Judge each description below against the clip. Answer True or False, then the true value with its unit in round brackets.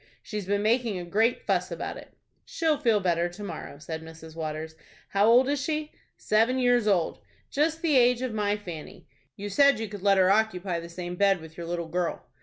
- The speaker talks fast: True (210 wpm)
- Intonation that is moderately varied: False (5.9 semitones)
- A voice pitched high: True (205 Hz)